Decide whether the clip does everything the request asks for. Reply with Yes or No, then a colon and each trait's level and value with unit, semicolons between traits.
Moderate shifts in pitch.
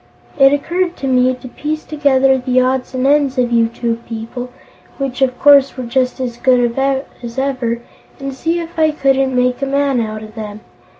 No: narrow, 2.2 semitones